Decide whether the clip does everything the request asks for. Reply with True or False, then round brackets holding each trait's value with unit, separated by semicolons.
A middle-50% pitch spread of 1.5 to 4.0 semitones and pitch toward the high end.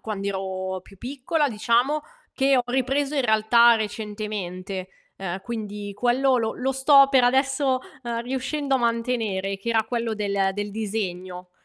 False (4.6 semitones; 230 Hz)